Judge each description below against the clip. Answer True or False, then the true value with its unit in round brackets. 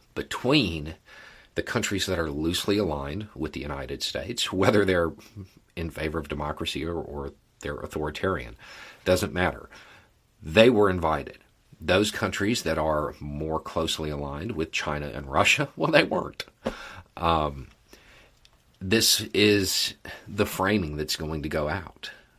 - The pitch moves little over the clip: False (5.0 semitones)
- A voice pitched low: True (80 Hz)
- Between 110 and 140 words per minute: True (135 wpm)